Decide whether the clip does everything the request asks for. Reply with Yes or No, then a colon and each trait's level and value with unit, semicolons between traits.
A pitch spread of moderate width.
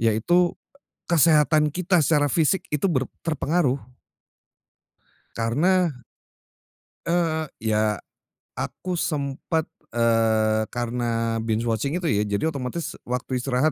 No: wide, 6.2 semitones